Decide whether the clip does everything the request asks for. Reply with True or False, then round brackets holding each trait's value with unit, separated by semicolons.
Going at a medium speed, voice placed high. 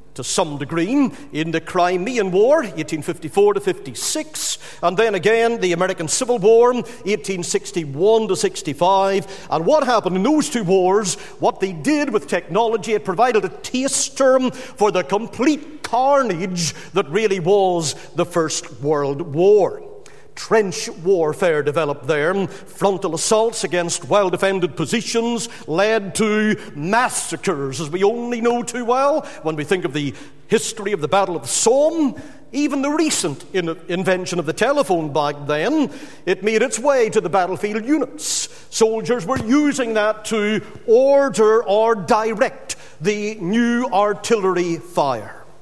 True (145 wpm; 210 Hz)